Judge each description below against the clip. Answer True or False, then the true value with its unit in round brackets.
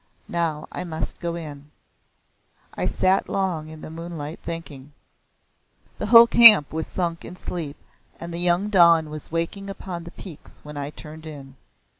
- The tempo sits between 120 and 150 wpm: False (160 wpm)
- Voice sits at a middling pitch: True (165 Hz)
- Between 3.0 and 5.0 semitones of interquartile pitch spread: False (2.6 semitones)